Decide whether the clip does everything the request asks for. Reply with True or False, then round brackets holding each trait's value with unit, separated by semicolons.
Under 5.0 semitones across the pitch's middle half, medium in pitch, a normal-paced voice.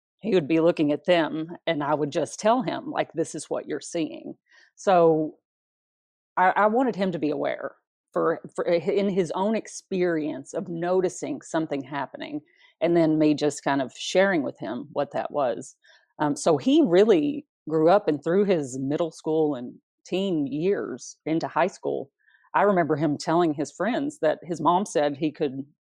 True (4.4 semitones; 170 Hz; 180 wpm)